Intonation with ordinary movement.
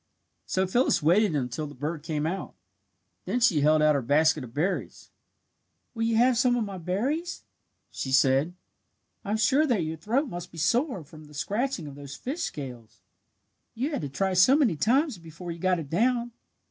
No: wide, 7.9 semitones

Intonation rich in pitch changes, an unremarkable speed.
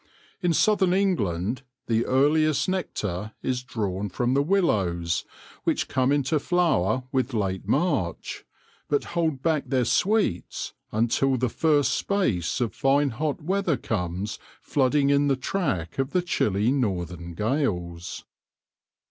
No: wide, 7.2 semitones; slow, 130 wpm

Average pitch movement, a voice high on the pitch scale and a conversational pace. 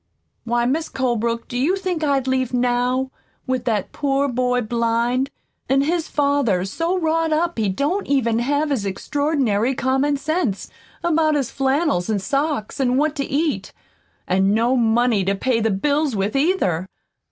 Yes: average, 4.0 semitones; very high, 260 Hz; average, 160 wpm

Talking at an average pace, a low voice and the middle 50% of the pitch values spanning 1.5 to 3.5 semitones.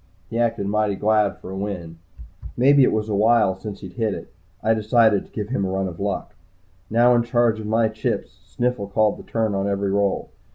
No: fast, 215 wpm; low, 105 Hz; narrow, 2.4 semitones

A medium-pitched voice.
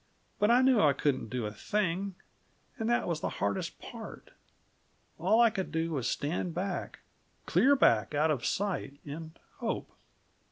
Yes: medium, 165 Hz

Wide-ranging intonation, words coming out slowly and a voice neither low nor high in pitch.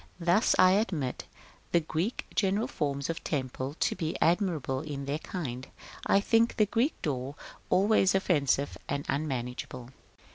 No: wide, 5.7 semitones; average, 145 wpm; medium, 155 Hz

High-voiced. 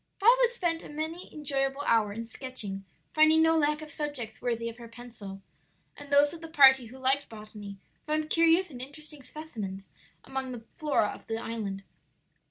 Yes: very high, 270 Hz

